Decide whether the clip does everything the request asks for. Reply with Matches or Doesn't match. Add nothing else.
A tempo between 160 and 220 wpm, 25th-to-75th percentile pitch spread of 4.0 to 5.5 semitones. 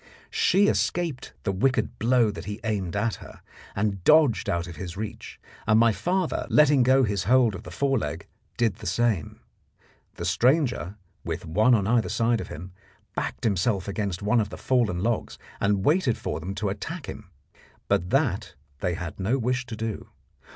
Matches